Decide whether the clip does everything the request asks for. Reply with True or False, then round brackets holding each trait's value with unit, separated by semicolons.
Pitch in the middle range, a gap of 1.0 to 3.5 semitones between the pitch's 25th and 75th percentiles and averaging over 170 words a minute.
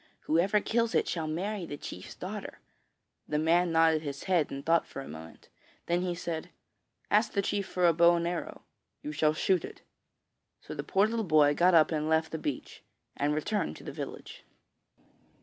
True (165 Hz; 3.1 semitones; 190 wpm)